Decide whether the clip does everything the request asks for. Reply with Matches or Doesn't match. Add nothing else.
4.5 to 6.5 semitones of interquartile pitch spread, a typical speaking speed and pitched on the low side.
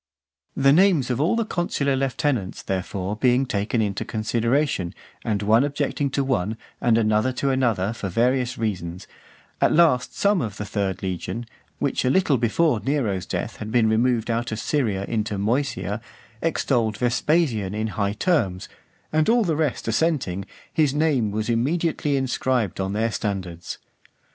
Matches